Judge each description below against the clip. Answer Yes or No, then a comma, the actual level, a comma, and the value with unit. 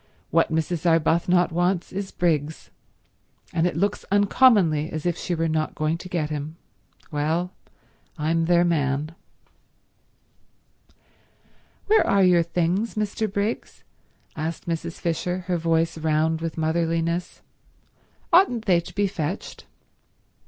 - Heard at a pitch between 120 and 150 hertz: No, medium, 170 Hz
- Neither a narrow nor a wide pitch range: No, narrow, 2.3 semitones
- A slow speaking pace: Yes, slow, 125 wpm